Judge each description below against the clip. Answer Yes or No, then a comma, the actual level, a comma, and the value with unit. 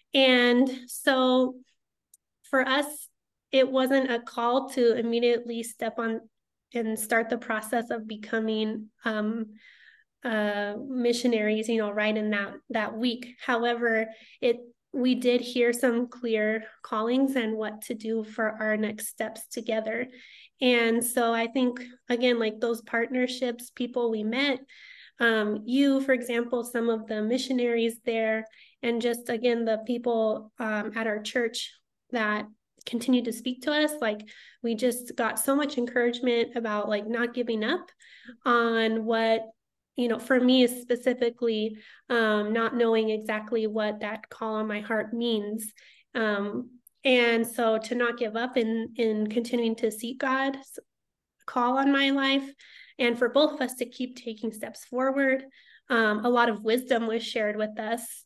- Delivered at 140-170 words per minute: Yes, average, 150 wpm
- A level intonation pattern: Yes, narrow, 2.1 semitones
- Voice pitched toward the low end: No, high, 235 Hz